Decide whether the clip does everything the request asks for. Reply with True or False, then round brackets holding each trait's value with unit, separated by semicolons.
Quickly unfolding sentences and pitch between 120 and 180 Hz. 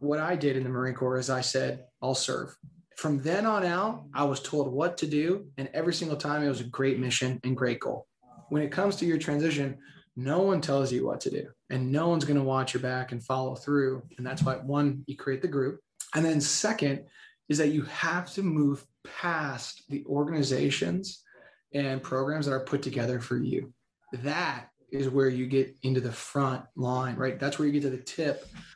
True (215 wpm; 140 Hz)